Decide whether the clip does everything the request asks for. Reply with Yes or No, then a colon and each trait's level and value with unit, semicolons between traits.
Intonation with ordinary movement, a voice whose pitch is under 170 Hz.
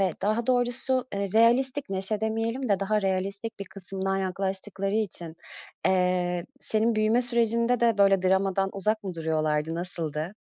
No: average, 3.3 semitones; high, 195 Hz